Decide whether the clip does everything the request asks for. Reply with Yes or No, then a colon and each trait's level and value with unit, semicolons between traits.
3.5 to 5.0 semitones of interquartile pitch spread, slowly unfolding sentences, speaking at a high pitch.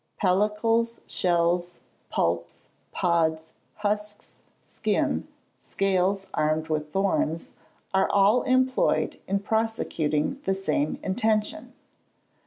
Yes: average, 4.0 semitones; slow, 85 wpm; high, 195 Hz